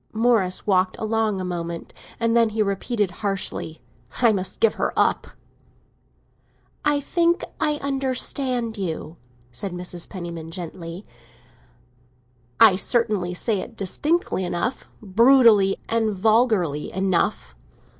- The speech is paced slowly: Yes, slow, 110 wpm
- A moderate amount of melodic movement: Yes, average, 4.5 semitones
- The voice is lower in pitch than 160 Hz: No, high, 205 Hz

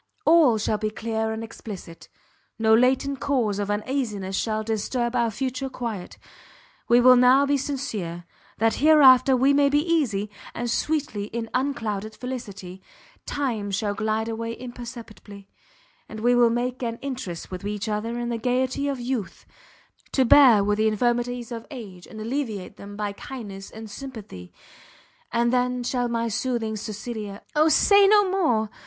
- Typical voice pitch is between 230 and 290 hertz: Yes, high, 235 Hz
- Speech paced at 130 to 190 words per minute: Yes, average, 160 wpm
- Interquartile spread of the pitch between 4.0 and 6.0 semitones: No, average, 3.4 semitones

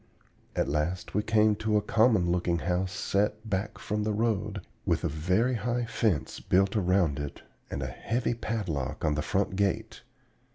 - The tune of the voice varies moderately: Yes, average, 3.8 semitones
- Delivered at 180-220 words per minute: No, average, 170 wpm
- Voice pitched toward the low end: Yes, low, 100 Hz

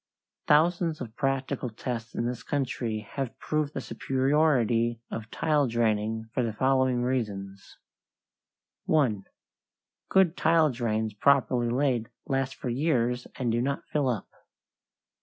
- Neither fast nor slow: No, slow, 125 wpm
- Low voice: Yes, low, 125 Hz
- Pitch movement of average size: Yes, average, 3.5 semitones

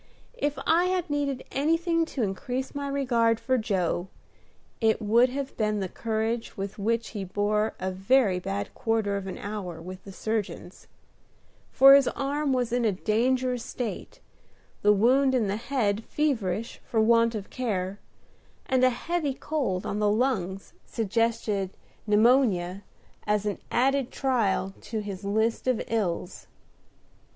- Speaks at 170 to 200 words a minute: No, average, 145 wpm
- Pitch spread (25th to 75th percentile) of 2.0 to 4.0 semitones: No, average, 4.4 semitones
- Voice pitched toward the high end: Yes, high, 225 Hz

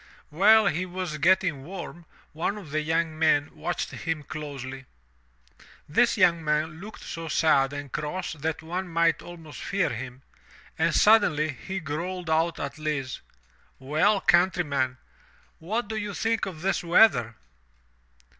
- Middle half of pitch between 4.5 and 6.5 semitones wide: No, average, 3.8 semitones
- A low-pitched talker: No, medium, 160 Hz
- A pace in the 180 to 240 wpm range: No, average, 140 wpm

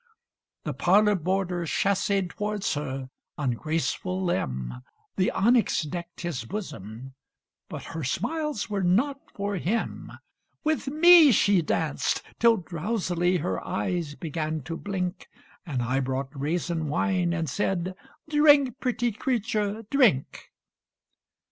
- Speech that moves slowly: Yes, slow, 120 wpm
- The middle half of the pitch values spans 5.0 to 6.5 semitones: Yes, wide, 5.6 semitones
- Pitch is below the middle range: No, medium, 180 Hz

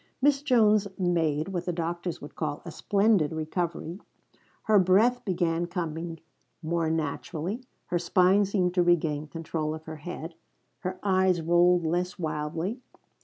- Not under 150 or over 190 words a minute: No, average, 140 wpm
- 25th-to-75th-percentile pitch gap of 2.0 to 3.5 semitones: Yes, average, 2.8 semitones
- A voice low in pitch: No, medium, 175 Hz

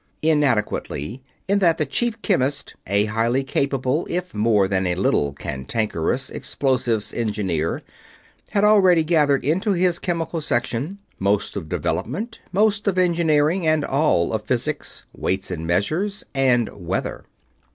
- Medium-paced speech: No, slow, 130 wpm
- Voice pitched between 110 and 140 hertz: Yes, low, 135 Hz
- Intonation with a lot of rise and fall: Yes, wide, 8.6 semitones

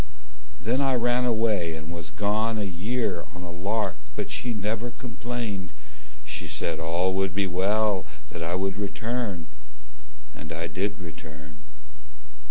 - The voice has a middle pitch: No, very low, 95 Hz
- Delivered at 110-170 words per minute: Yes, average, 145 wpm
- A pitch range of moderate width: Yes, average, 4.5 semitones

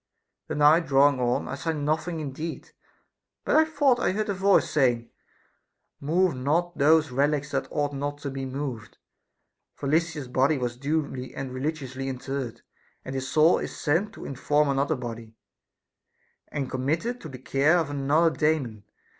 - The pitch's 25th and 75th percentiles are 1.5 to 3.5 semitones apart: Yes, average, 3.2 semitones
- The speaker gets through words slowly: No, average, 160 wpm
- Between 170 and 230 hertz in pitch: No, medium, 145 Hz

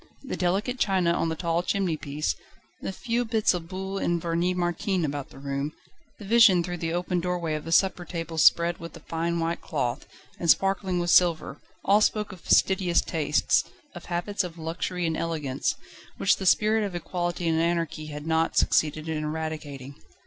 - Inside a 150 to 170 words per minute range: No, average, 185 wpm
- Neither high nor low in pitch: Yes, medium, 170 Hz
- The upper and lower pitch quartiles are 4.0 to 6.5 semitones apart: No, narrow, 2.6 semitones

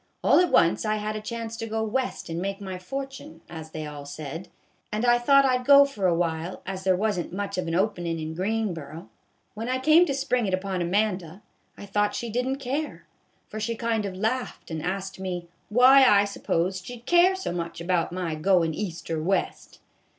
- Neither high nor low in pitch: No, high, 200 Hz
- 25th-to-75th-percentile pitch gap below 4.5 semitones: No, wide, 5.4 semitones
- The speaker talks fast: Yes, fast, 220 wpm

